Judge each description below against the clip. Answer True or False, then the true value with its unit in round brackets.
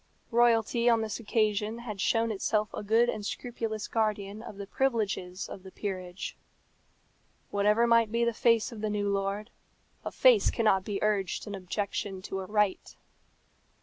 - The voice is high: True (215 Hz)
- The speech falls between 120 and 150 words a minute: False (160 wpm)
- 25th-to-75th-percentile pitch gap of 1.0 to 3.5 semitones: True (2.4 semitones)